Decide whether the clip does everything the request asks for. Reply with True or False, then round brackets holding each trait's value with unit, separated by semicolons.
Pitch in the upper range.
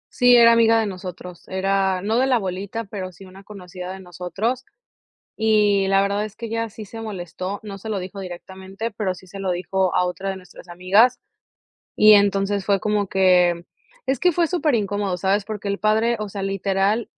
True (195 Hz)